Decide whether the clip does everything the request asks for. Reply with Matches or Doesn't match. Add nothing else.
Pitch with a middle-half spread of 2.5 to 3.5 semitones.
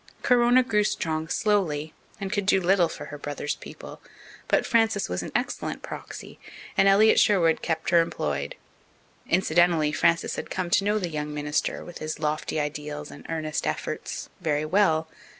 Doesn't match